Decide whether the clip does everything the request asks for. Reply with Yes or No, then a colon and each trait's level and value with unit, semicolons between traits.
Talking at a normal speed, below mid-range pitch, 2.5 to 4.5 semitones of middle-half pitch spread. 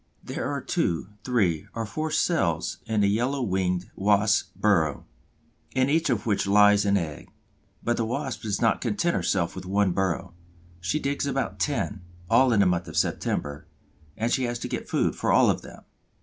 No: average, 185 wpm; low, 105 Hz; average, 5.0 semitones